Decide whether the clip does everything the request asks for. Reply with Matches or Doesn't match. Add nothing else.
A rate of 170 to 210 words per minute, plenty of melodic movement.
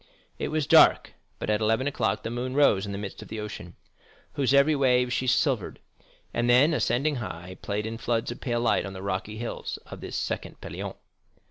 Doesn't match